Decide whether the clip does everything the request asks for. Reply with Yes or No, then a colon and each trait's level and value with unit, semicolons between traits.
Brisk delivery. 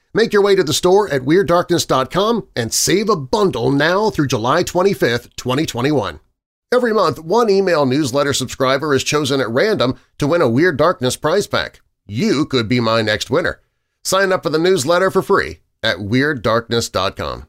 No: average, 170 wpm